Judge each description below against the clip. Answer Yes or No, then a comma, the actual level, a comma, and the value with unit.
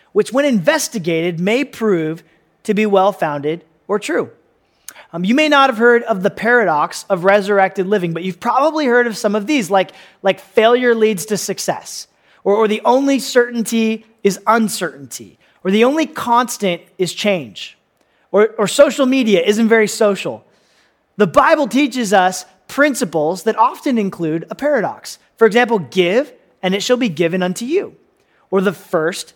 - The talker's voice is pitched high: Yes, high, 210 Hz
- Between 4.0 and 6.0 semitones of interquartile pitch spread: Yes, average, 4.4 semitones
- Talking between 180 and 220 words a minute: No, average, 165 wpm